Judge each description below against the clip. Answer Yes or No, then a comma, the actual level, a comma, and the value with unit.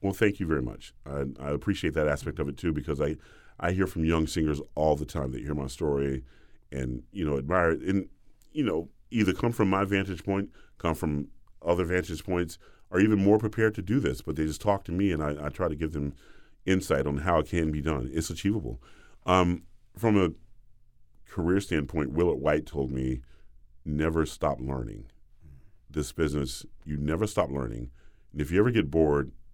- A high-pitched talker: No, very low, 80 Hz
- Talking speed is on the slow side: No, average, 200 wpm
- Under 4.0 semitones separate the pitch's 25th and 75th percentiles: No, average, 5.0 semitones